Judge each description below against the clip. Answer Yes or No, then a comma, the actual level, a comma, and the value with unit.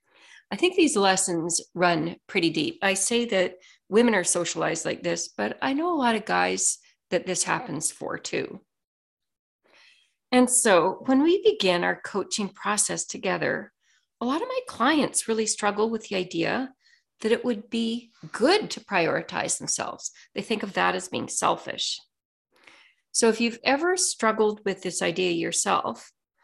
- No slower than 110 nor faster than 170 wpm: Yes, average, 160 wpm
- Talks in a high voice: Yes, high, 220 Hz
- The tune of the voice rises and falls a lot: Yes, wide, 6.1 semitones